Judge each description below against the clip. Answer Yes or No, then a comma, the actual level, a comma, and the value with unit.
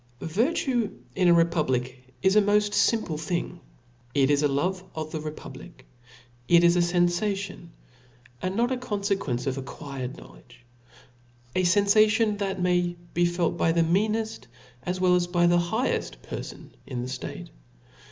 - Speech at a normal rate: Yes, average, 160 wpm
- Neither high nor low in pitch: Yes, medium, 175 Hz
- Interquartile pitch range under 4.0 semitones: No, average, 4.4 semitones